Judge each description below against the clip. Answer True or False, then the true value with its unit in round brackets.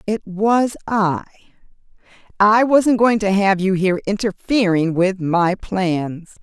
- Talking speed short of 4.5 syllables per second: True (3.7 syllables/s)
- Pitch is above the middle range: True (200 Hz)